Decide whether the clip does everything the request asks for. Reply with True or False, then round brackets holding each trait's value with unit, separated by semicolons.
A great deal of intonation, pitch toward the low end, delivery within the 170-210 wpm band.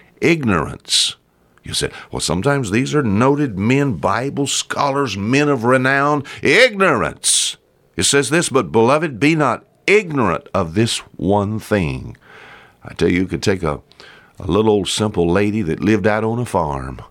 False (6.4 semitones; 110 Hz; 160 wpm)